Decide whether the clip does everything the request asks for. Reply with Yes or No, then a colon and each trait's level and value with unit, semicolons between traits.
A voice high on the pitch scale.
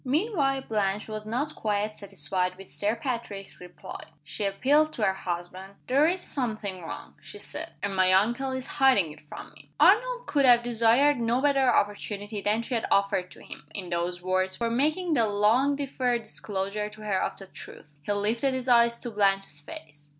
Yes: high, 215 Hz